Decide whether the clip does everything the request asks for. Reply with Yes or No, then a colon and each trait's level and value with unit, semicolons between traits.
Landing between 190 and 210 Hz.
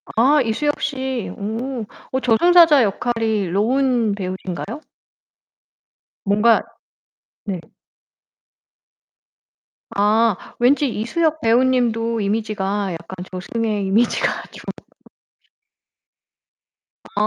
No: high, 225 Hz